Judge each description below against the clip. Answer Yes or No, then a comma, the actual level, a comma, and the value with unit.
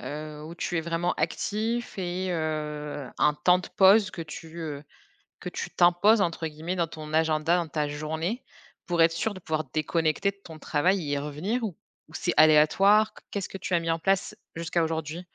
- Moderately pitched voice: Yes, medium, 165 Hz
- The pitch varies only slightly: No, average, 3.0 semitones